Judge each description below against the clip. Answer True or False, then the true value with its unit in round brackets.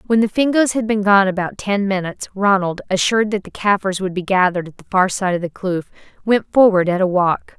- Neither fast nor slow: False (230 wpm)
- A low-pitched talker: False (195 Hz)